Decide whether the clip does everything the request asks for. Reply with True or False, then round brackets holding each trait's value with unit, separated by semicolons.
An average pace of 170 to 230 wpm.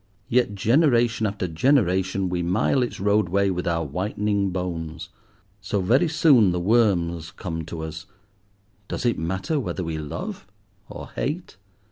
False (140 wpm)